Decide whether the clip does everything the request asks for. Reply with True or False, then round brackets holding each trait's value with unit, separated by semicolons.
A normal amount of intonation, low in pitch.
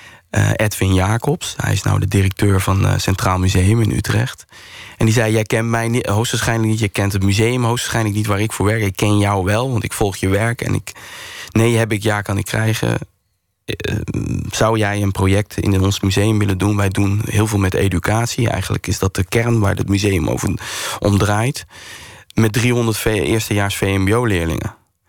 False (2.3 semitones; 105 Hz)